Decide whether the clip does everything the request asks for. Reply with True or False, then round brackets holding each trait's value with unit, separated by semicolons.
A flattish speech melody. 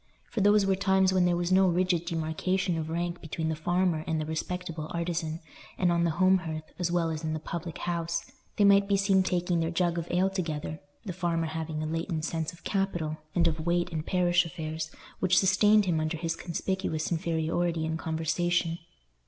True (2.3 semitones)